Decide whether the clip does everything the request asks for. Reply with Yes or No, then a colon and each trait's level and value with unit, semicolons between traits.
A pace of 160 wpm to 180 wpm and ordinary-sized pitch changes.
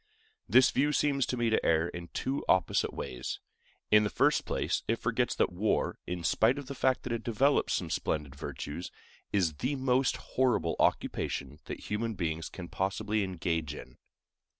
No: average, 175 wpm; wide, 7.4 semitones